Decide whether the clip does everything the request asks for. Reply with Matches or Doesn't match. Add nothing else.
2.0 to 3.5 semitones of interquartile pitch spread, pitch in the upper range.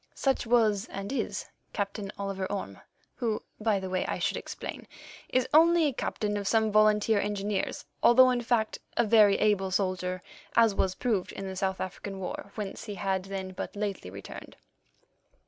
Matches